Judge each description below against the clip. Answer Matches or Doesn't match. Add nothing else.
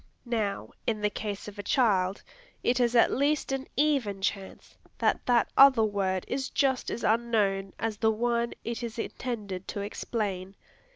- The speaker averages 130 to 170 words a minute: Matches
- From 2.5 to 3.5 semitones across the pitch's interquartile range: Matches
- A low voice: Doesn't match